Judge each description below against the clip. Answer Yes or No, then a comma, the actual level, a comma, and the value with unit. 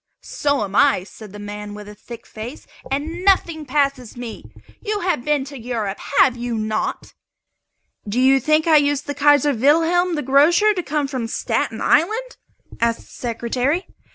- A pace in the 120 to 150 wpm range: No, average, 170 wpm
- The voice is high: Yes, very high, 275 Hz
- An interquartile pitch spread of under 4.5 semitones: No, average, 5.0 semitones